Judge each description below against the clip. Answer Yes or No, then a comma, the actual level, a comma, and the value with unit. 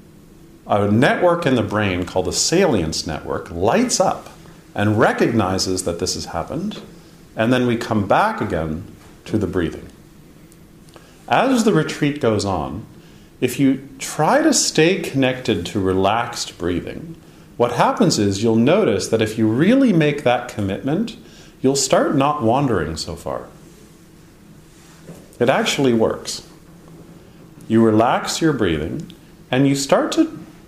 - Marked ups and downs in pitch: Yes, wide, 7.7 semitones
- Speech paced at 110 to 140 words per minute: Yes, slow, 135 wpm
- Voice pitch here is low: Yes, low, 125 Hz